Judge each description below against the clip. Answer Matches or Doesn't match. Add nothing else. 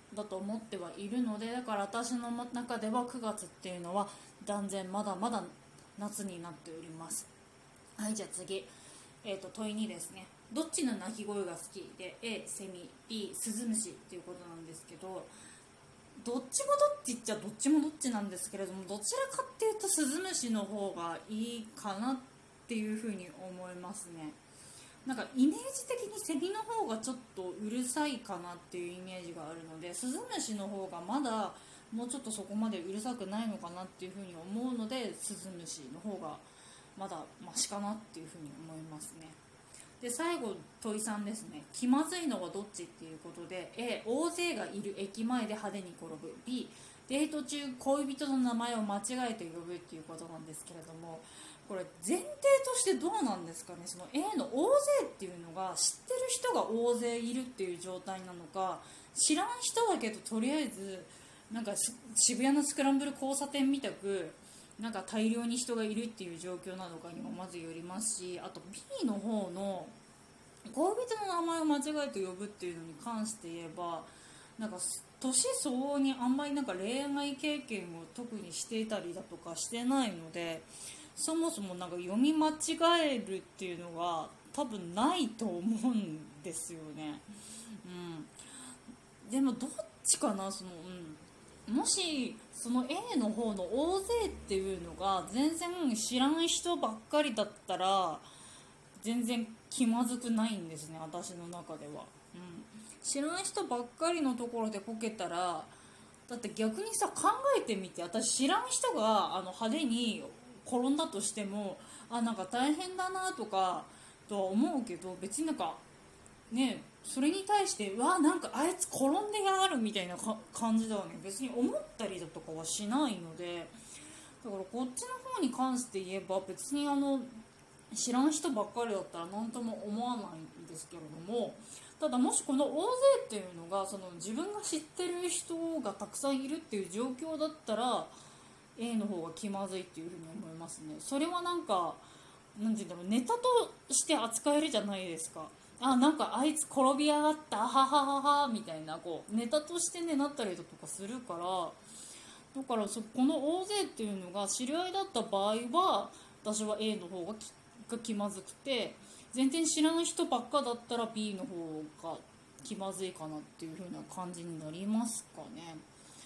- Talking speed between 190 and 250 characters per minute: Doesn't match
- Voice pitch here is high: Matches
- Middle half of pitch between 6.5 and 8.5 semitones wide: Matches